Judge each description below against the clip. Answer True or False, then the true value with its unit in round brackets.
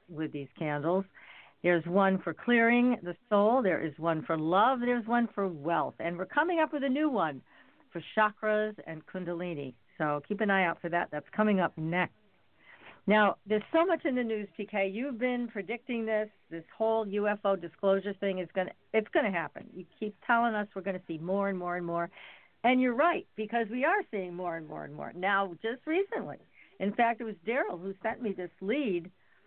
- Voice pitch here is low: False (200 Hz)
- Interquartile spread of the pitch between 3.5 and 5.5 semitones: True (4.7 semitones)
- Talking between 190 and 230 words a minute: True (205 wpm)